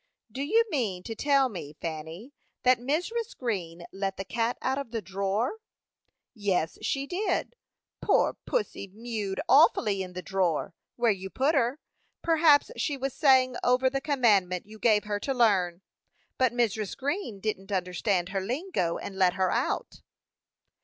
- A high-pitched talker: Yes, high, 225 Hz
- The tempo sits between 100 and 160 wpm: Yes, average, 155 wpm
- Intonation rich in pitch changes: Yes, wide, 5.9 semitones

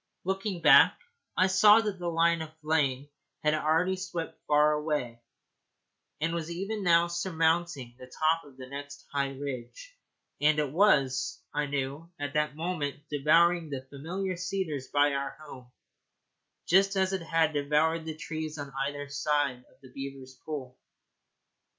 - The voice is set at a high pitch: No, medium, 155 Hz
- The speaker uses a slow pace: No, average, 150 wpm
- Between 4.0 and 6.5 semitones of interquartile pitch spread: No, average, 3.4 semitones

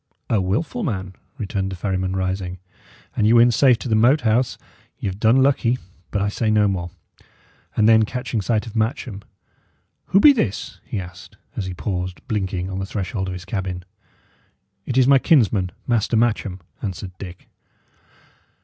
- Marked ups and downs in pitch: No, average, 4.0 semitones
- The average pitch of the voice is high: No, low, 105 Hz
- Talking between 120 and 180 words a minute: Yes, average, 170 wpm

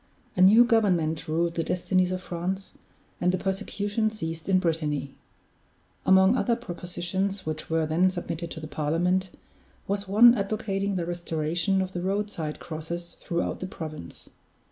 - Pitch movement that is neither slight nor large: Yes, average, 3.1 semitones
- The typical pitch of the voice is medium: Yes, medium, 180 Hz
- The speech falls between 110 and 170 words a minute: Yes, average, 150 wpm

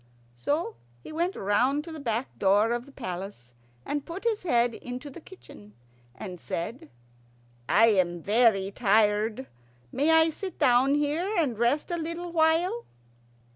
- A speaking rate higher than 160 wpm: No, average, 150 wpm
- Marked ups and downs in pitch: Yes, wide, 7.6 semitones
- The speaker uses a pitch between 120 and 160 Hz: No, very high, 255 Hz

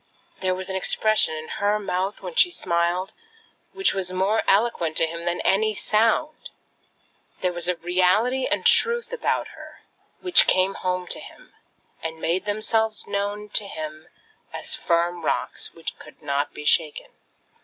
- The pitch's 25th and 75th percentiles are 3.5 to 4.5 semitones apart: Yes, average, 4.0 semitones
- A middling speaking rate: Yes, average, 160 wpm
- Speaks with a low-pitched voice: No, high, 190 Hz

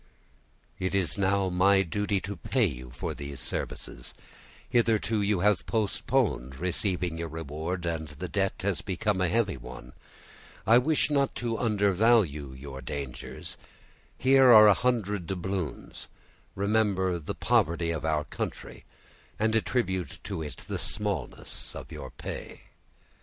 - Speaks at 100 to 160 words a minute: Yes, slow, 135 wpm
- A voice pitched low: Yes, very low, 95 Hz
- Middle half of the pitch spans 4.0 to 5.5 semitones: Yes, average, 4.9 semitones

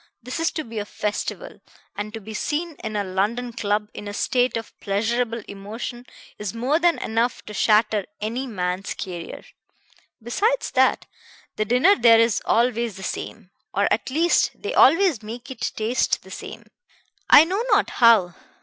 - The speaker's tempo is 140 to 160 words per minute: No, average, 170 wpm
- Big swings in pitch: No, average, 3.3 semitones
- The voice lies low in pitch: No, high, 230 Hz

